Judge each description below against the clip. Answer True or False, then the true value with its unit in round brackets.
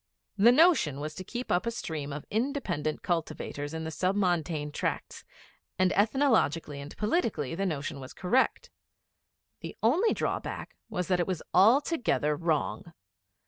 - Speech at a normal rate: True (145 wpm)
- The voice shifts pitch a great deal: True (6.7 semitones)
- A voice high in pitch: False (175 Hz)